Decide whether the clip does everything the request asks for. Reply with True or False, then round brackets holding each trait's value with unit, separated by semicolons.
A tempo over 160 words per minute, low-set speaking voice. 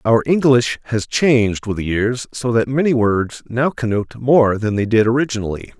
True (185 wpm; 120 Hz)